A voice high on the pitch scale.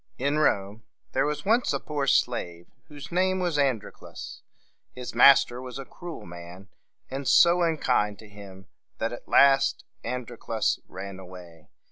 No: low, 125 Hz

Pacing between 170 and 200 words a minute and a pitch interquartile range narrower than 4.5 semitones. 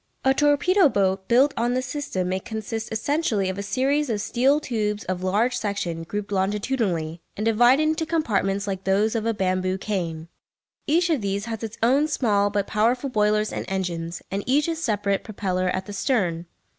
No: average, 180 wpm; average, 5.0 semitones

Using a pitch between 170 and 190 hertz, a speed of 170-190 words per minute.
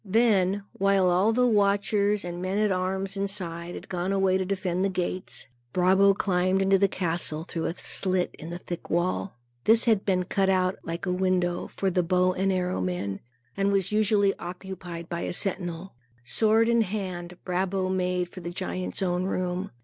Yes: medium, 185 Hz; average, 180 wpm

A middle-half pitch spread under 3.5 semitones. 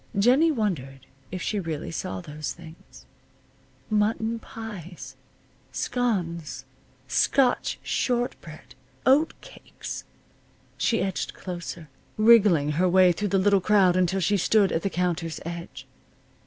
No: average, 4.5 semitones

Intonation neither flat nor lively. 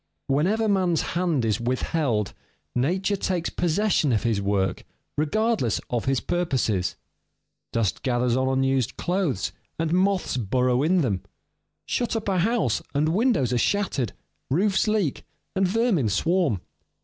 No: wide, 7.6 semitones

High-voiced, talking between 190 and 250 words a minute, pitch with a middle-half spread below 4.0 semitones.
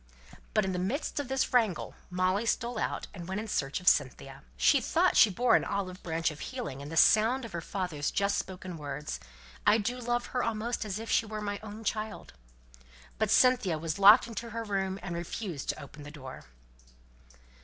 No: high, 200 Hz; average, 200 wpm; average, 5.0 semitones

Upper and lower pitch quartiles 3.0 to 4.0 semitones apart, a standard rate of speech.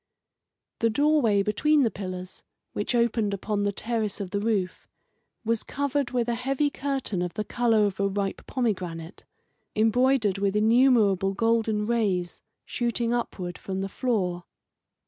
Yes: average, 3.5 semitones; average, 145 wpm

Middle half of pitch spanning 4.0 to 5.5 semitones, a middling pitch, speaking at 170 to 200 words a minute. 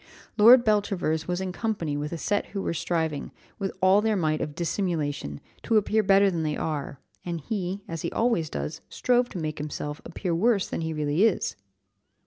Yes: average, 4.9 semitones; medium, 175 Hz; average, 190 wpm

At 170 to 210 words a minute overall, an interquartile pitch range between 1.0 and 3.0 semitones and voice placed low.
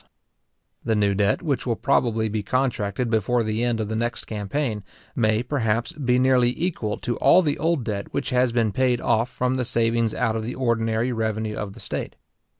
Yes: average, 200 wpm; narrow, 2.5 semitones; low, 115 Hz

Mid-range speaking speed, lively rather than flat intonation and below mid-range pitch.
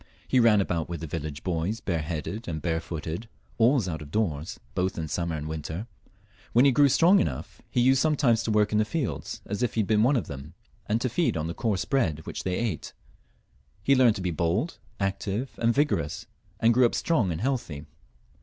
No: fast, 210 wpm; wide, 6.6 semitones; low, 100 Hz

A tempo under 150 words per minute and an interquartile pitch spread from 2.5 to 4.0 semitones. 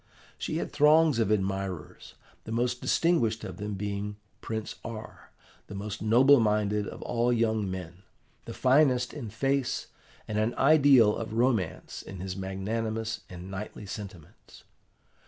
Yes: average, 140 wpm; average, 3.5 semitones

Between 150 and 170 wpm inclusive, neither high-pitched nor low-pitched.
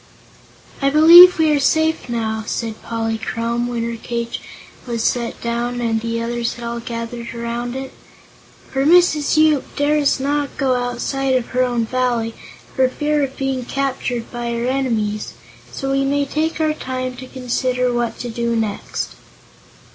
No: average, 160 wpm; high, 245 Hz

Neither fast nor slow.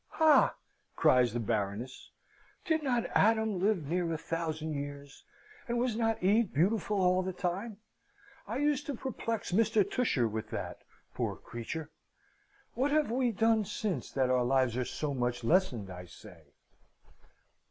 Yes: average, 150 wpm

